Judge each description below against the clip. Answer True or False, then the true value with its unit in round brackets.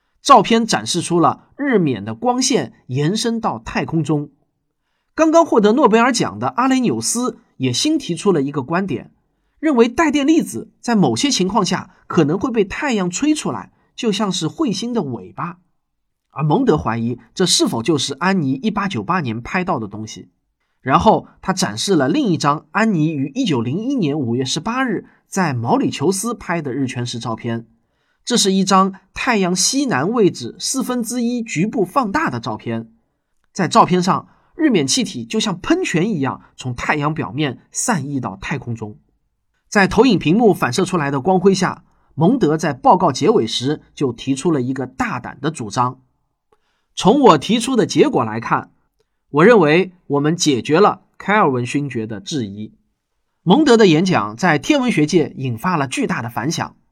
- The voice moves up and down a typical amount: False (8.4 semitones)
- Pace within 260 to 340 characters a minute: False (245 characters per minute)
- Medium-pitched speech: True (175 Hz)